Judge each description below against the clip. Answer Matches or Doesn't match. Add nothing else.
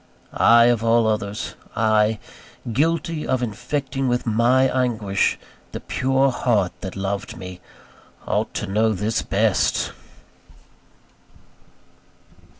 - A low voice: Matches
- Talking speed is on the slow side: Matches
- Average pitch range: Matches